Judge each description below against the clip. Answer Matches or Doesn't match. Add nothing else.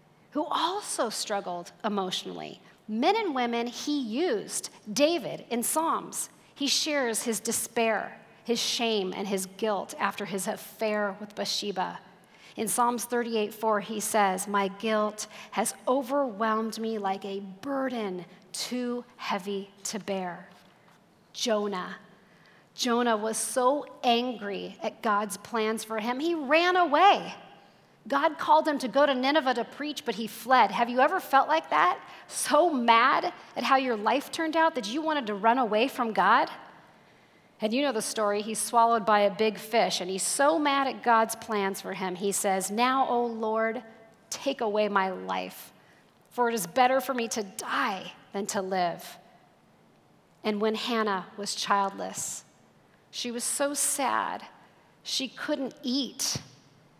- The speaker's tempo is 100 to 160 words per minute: Matches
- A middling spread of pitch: Matches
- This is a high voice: Matches